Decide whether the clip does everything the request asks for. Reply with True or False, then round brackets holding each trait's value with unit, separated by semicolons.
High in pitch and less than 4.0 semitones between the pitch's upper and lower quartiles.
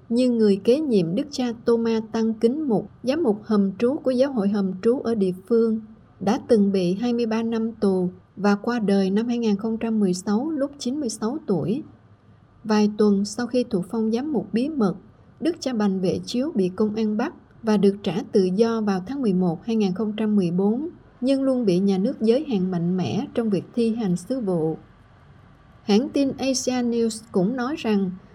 True (220 Hz; 3.4 semitones)